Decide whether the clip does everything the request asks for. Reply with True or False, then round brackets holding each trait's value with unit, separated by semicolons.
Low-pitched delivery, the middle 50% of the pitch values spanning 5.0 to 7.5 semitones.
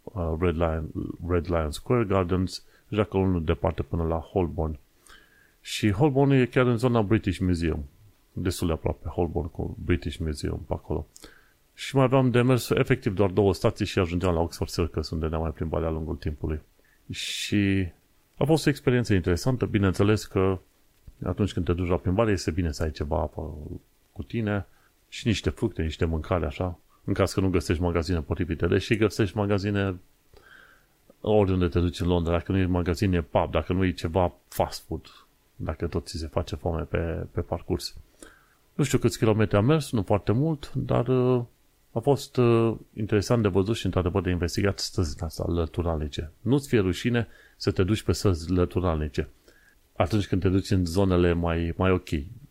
False (95 Hz; 3.9 semitones)